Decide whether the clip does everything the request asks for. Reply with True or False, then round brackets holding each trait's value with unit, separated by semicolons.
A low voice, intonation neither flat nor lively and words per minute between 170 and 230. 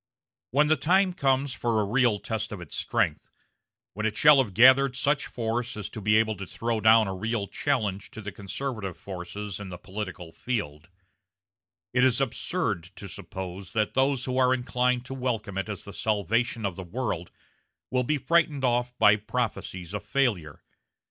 True (110 Hz; 4.3 semitones; 180 wpm)